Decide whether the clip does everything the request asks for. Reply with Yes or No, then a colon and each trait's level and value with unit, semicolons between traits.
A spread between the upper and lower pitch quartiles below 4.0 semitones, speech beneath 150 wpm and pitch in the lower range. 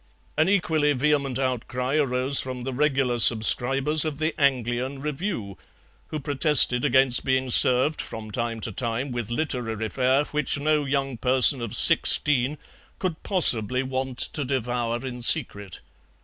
Yes: average, 3.2 semitones; average, 140 wpm; low, 130 Hz